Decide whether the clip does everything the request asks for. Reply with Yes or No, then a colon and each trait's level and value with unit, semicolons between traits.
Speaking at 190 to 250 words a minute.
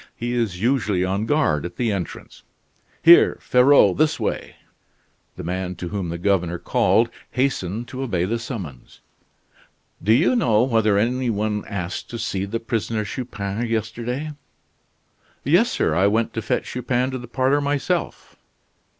No: average, 150 wpm